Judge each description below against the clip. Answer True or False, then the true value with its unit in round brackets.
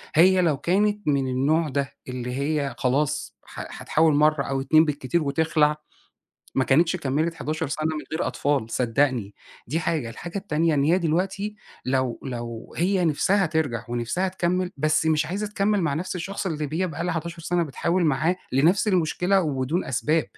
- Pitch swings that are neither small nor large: True (4.1 semitones)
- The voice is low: False (155 Hz)